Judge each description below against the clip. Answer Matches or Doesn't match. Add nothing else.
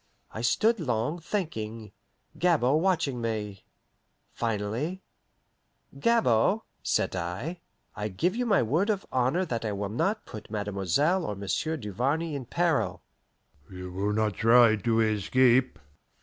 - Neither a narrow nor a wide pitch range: Doesn't match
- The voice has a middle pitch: Doesn't match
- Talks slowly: Matches